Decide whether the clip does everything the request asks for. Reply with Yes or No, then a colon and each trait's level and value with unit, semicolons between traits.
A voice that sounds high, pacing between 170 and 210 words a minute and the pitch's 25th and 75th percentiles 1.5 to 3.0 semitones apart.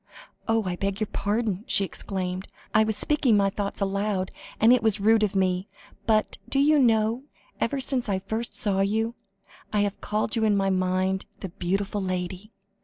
Yes: high, 205 Hz; average, 180 wpm; narrow, 2.5 semitones